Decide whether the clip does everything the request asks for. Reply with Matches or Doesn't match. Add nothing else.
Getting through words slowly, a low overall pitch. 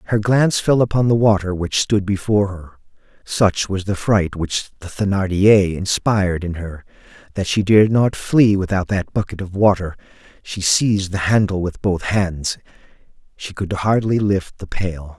Doesn't match